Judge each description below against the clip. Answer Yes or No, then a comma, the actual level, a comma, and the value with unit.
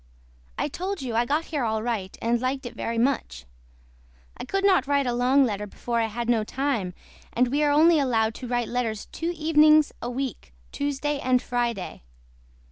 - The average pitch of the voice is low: No, very high, 250 Hz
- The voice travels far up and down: No, average, 3.8 semitones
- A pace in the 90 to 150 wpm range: No, average, 190 wpm